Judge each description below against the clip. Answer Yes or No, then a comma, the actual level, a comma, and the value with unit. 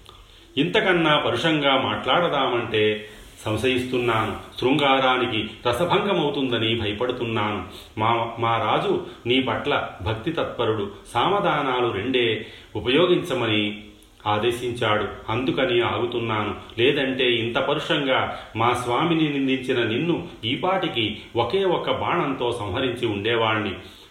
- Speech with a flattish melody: No, average, 3.6 semitones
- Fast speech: No, average, 80 wpm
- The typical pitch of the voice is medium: No, low, 120 Hz